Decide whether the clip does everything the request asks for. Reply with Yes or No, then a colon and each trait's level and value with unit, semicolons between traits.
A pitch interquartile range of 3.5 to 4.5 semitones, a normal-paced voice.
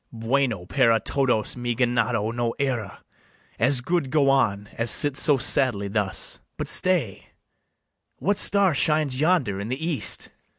Yes: average, 4.2 semitones; average, 145 wpm